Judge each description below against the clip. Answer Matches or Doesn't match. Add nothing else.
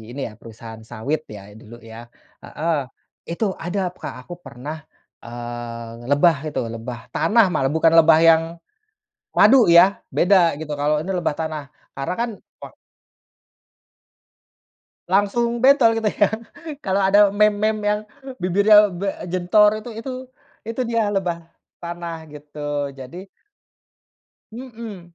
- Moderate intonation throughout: Doesn't match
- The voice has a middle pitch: Matches